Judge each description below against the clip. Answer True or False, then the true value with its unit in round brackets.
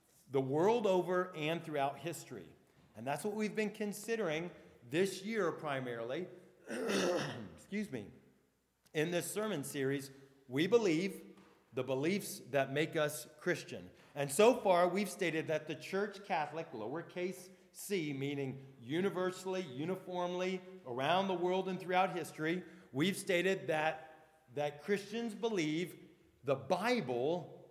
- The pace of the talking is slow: True (125 wpm)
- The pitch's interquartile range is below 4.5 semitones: True (3.7 semitones)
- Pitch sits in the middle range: True (175 Hz)